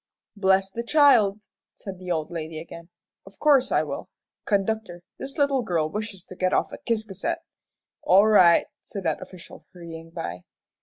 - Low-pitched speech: No, high, 195 Hz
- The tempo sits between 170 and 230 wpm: No, average, 160 wpm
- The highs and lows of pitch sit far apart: No, average, 4.3 semitones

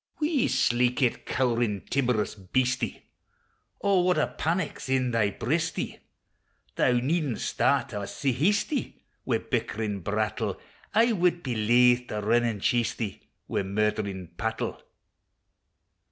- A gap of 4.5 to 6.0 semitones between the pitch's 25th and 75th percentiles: Yes, wide, 5.5 semitones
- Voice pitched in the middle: No, low, 120 Hz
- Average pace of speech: No, slow, 125 wpm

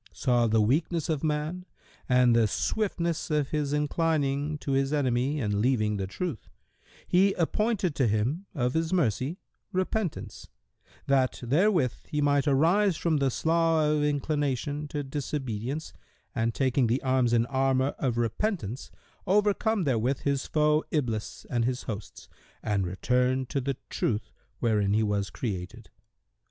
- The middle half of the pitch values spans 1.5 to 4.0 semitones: No, average, 4.7 semitones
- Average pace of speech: Yes, average, 145 wpm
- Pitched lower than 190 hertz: Yes, low, 135 Hz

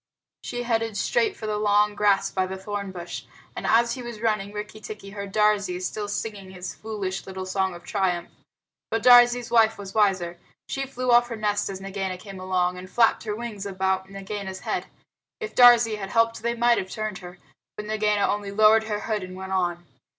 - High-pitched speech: Yes, high, 205 Hz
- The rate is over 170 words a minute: Yes, average, 200 wpm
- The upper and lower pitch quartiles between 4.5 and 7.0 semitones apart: No, average, 2.8 semitones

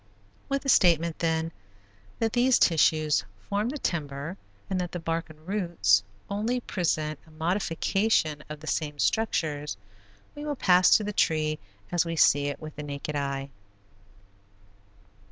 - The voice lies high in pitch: No, medium, 165 Hz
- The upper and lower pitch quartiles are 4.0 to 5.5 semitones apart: Yes, average, 4.7 semitones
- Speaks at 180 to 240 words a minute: No, average, 150 wpm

